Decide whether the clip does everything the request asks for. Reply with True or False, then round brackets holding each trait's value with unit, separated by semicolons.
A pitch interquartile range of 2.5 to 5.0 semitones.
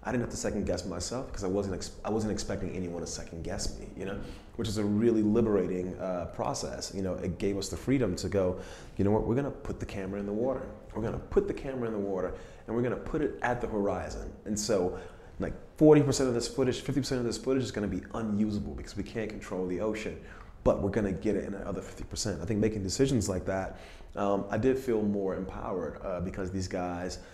True (3.3 semitones)